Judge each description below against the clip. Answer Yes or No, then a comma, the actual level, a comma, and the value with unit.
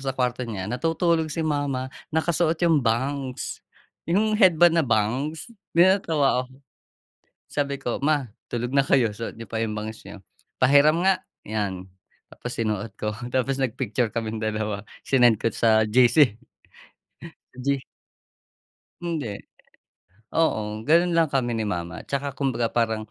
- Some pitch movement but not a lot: No, wide, 5.7 semitones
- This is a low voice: Yes, low, 130 Hz